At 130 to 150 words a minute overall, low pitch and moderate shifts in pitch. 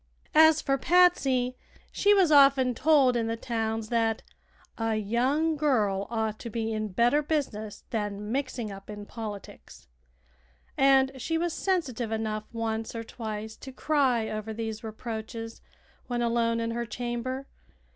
No: average, 145 wpm; high, 235 Hz; average, 3.5 semitones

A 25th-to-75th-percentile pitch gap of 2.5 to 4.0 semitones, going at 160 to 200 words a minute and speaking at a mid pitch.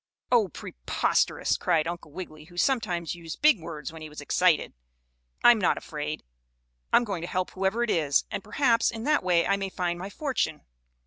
No: average, 5.1 semitones; average, 185 wpm; medium, 180 Hz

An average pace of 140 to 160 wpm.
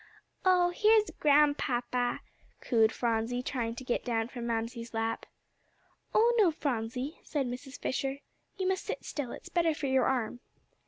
Yes: average, 150 wpm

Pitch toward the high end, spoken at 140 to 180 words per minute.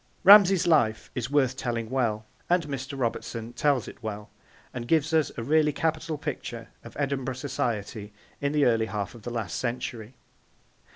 No: low, 125 Hz; average, 165 wpm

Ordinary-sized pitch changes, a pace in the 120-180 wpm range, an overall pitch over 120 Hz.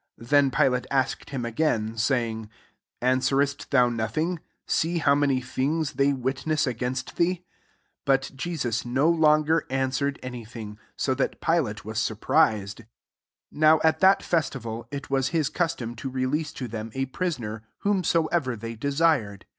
Yes: average, 4.7 semitones; average, 160 wpm; low, 135 Hz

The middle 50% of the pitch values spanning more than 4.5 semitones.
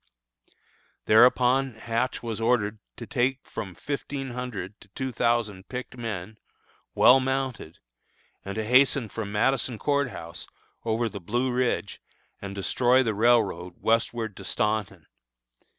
No: average, 3.6 semitones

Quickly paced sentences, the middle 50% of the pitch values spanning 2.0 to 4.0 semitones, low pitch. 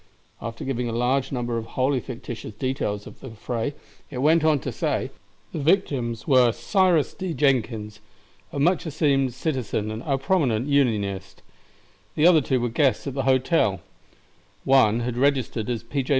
No: average, 165 wpm; average, 3.7 semitones; low, 130 Hz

